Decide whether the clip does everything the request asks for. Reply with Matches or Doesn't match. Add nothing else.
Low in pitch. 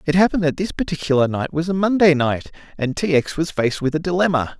Doesn't match